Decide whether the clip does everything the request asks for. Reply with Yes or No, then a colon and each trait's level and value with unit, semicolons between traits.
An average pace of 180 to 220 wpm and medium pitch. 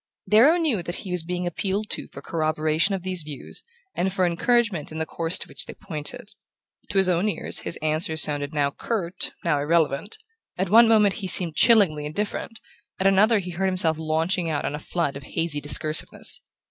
Yes: average, 195 wpm; medium, 175 Hz